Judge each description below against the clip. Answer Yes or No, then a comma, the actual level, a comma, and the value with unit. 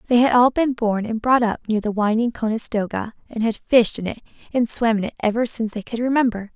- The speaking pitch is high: Yes, high, 230 Hz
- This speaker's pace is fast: Yes, fast, 240 wpm